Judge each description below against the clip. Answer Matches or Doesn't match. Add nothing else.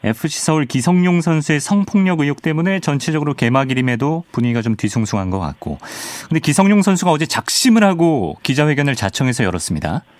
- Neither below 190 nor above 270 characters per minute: Doesn't match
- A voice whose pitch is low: Doesn't match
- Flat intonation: Doesn't match